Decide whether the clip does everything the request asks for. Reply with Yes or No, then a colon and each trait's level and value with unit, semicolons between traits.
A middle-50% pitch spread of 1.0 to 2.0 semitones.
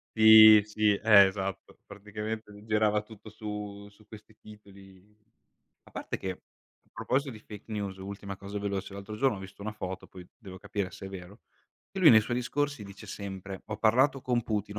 Yes: narrow, 1.7 semitones